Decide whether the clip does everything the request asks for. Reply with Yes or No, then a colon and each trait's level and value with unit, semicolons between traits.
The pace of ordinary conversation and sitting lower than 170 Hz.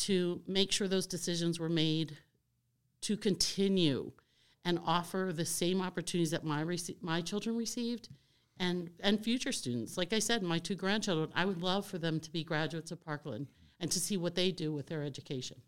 No: average, 190 wpm; medium, 175 Hz